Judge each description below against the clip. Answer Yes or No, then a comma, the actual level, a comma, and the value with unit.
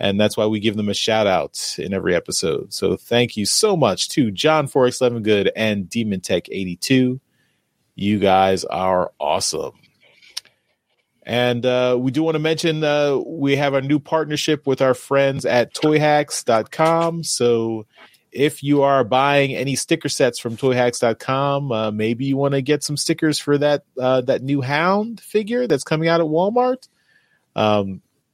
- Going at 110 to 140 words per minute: No, average, 165 wpm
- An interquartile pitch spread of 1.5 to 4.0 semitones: No, average, 4.7 semitones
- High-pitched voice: No, low, 135 Hz